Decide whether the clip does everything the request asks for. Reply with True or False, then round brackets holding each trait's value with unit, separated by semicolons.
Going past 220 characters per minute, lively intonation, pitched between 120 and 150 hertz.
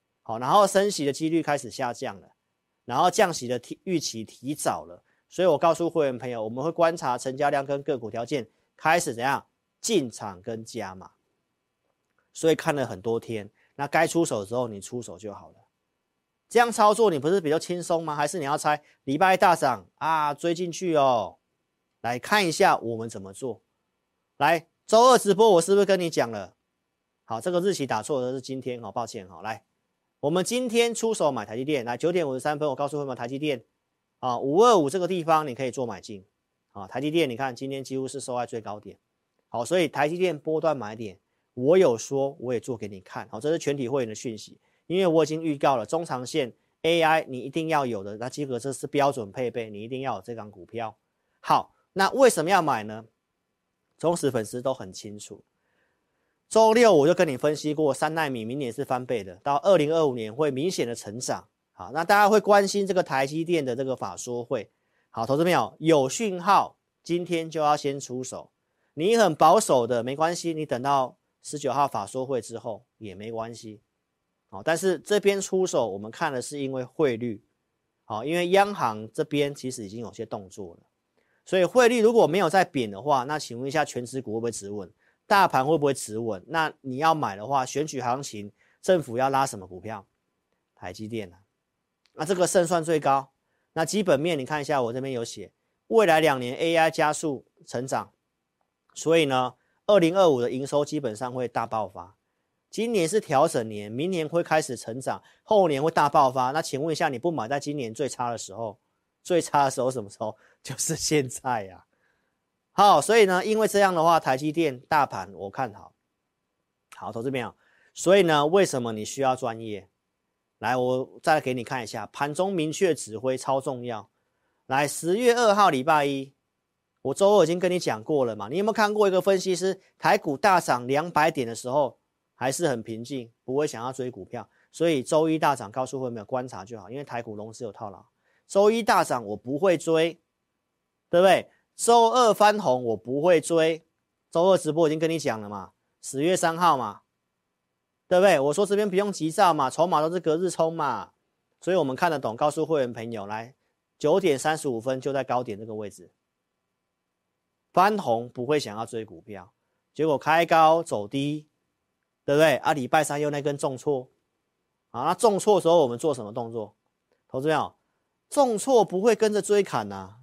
True (285 characters per minute; 6.0 semitones; 140 Hz)